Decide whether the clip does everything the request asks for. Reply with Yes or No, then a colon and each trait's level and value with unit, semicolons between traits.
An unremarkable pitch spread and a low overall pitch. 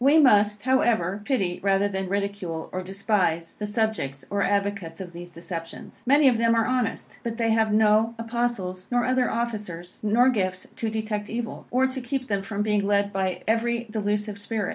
No: average, 3.2 semitones; high, 210 Hz